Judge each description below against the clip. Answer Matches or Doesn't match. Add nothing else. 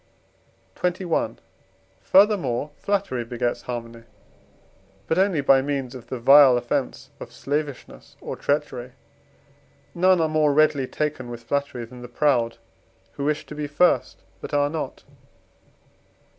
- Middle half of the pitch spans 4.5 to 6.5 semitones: Doesn't match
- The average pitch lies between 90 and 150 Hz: Matches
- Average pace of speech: Doesn't match